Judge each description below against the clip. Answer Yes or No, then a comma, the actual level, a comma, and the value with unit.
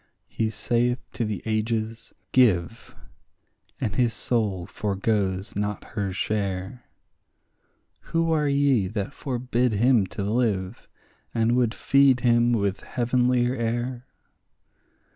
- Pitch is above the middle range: No, low, 115 Hz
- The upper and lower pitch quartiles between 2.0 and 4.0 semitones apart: Yes, average, 3.3 semitones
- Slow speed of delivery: Yes, slow, 110 wpm